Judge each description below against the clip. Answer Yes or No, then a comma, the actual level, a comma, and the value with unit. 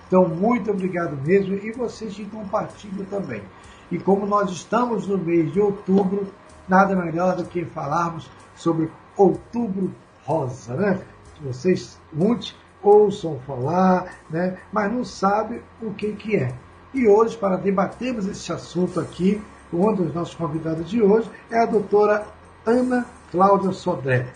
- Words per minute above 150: No, average, 140 wpm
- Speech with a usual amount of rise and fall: Yes, average, 3.7 semitones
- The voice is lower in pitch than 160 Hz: No, high, 195 Hz